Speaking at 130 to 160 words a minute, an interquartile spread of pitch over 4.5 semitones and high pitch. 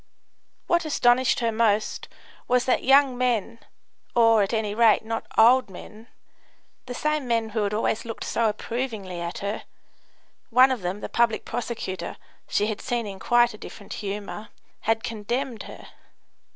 No: average, 150 wpm; average, 2.7 semitones; high, 225 Hz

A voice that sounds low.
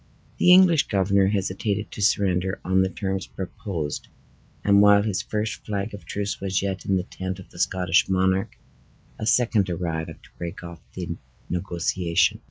Yes: very low, 95 Hz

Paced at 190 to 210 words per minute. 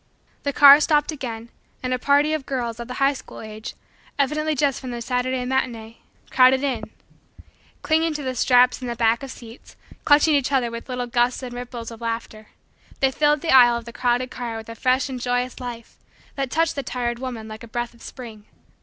Yes: fast, 205 wpm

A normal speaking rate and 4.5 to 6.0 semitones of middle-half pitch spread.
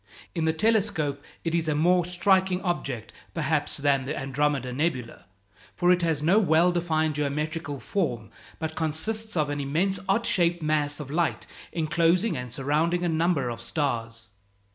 No: average, 160 wpm; average, 3.6 semitones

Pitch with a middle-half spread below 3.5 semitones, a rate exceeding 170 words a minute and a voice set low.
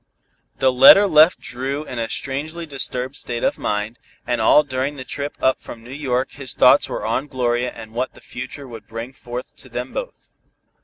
Yes: average, 2.8 semitones; average, 195 wpm; low, 130 Hz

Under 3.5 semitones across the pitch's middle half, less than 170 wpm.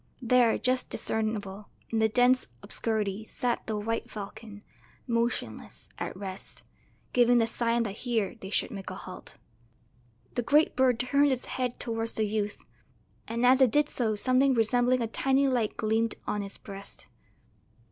Yes: average, 2.7 semitones; average, 155 wpm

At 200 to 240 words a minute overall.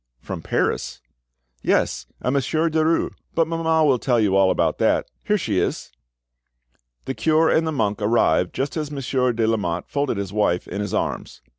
No: average, 175 wpm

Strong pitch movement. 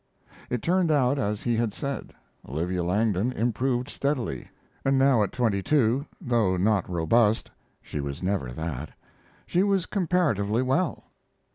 Yes: wide, 6.5 semitones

